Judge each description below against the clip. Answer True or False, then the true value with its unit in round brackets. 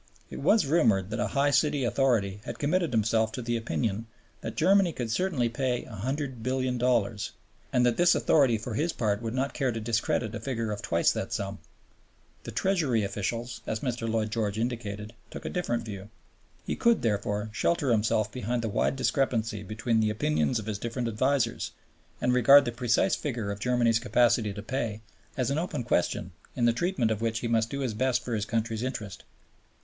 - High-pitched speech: False (115 Hz)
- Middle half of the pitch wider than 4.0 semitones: False (3.1 semitones)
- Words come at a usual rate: True (190 wpm)